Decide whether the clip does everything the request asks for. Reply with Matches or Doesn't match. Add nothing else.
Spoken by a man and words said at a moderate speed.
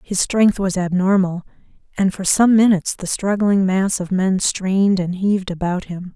Doesn't match